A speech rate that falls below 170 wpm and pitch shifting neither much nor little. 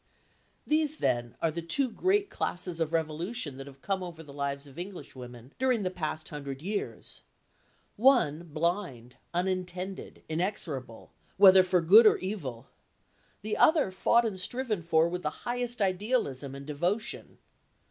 No: average, 145 wpm; wide, 6.0 semitones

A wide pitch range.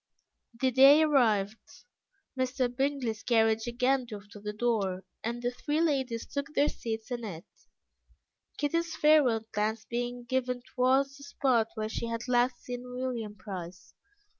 No: average, 3.1 semitones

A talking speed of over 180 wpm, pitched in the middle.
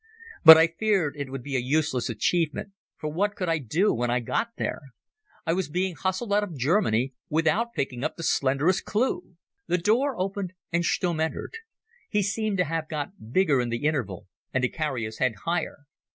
Yes: average, 195 wpm; medium, 160 Hz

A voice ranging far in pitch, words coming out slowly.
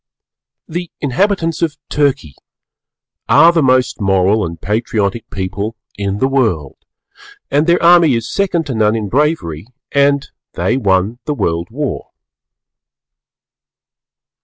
Yes: wide, 7.1 semitones; slow, 120 wpm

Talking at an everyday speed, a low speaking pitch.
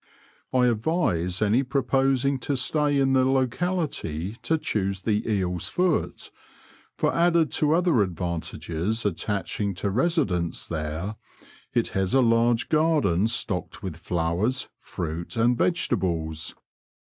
No: slow, 120 wpm; low, 110 Hz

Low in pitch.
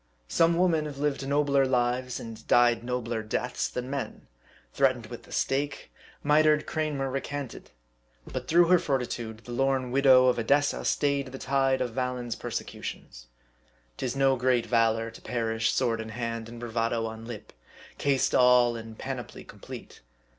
Yes: low, 125 Hz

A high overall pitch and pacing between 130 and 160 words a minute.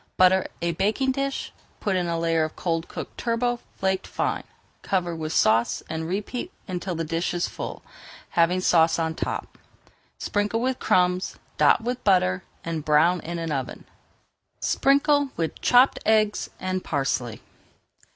No: medium, 180 Hz; average, 150 wpm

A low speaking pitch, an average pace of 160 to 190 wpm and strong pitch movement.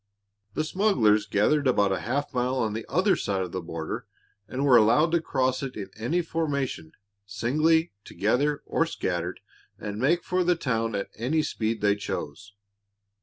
Yes: low, 125 Hz; average, 170 wpm; wide, 6.9 semitones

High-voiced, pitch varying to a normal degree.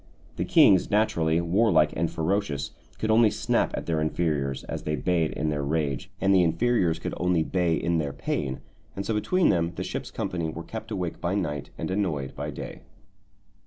No: very low, 85 Hz; average, 3.9 semitones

